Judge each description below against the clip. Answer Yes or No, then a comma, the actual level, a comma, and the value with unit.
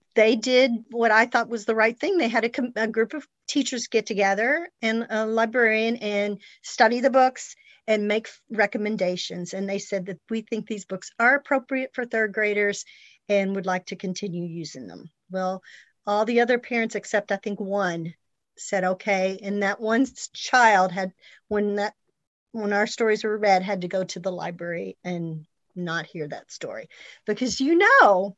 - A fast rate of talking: No, average, 185 wpm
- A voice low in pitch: No, high, 210 Hz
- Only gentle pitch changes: No, average, 3.2 semitones